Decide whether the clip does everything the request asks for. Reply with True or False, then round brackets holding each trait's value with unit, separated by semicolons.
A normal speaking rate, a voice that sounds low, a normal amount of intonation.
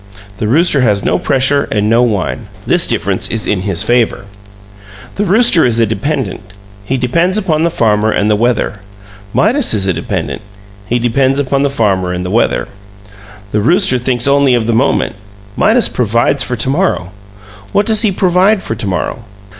False (180 wpm; 125 Hz; 6.5 semitones)